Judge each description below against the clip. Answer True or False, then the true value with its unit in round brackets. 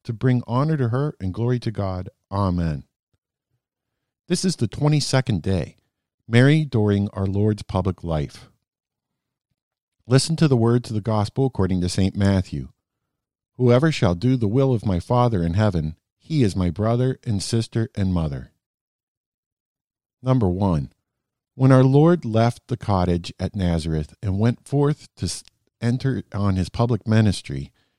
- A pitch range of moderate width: True (5.0 semitones)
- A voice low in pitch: True (110 Hz)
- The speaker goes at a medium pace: True (150 wpm)